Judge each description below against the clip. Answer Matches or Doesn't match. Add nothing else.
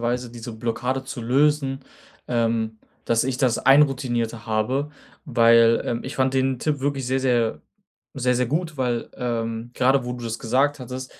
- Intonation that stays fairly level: Matches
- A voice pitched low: Matches